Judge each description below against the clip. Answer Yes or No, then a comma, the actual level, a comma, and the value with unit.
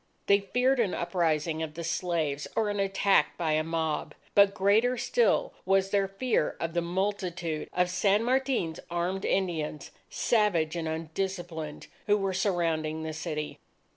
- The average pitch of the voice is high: No, medium, 175 Hz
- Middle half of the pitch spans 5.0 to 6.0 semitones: No, average, 3.8 semitones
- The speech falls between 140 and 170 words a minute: Yes, average, 150 wpm